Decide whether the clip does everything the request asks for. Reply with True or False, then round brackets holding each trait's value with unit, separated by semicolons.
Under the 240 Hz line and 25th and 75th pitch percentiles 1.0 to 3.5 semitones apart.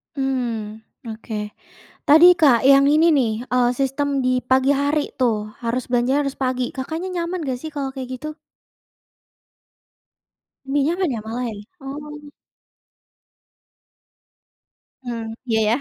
False (265 Hz; 3.0 semitones)